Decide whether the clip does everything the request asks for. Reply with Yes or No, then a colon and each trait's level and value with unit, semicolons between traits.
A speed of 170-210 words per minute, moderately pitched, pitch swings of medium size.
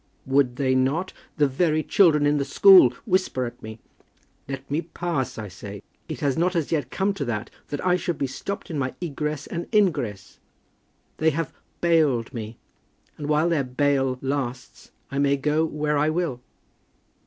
Yes: average, 175 wpm; medium, 145 Hz; average, 4.1 semitones